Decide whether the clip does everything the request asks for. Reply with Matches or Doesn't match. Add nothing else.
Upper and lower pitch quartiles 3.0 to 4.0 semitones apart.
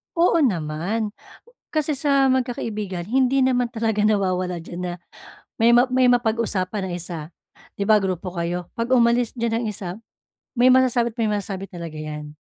Doesn't match